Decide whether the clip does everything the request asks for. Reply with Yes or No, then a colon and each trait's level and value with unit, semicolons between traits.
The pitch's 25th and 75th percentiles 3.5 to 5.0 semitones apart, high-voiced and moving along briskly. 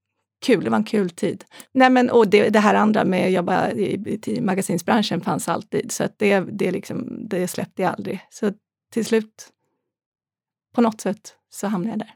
No: average, 3.1 semitones; high, 210 Hz; fast, 200 wpm